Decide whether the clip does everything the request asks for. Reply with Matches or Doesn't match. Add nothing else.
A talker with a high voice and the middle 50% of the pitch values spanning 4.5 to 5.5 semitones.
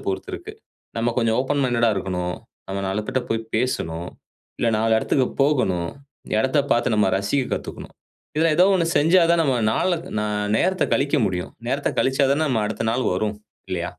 Doesn't match